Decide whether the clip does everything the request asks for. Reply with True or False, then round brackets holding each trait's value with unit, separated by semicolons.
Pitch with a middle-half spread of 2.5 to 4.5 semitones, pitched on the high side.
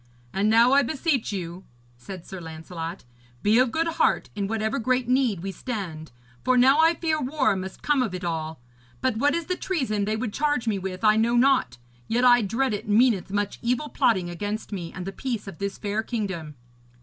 False (5.1 semitones; 220 Hz)